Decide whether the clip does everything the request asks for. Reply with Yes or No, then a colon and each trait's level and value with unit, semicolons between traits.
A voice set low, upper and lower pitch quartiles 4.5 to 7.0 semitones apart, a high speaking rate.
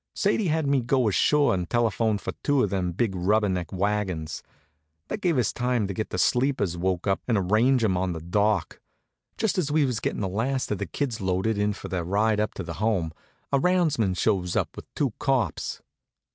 Yes: low, 105 Hz; average, 5.3 semitones; fast, 210 wpm